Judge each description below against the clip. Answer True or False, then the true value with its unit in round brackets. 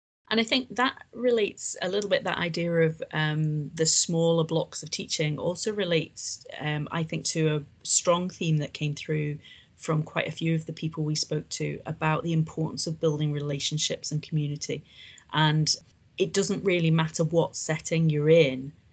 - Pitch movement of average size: False (2.0 semitones)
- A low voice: False (160 Hz)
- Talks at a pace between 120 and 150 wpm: False (180 wpm)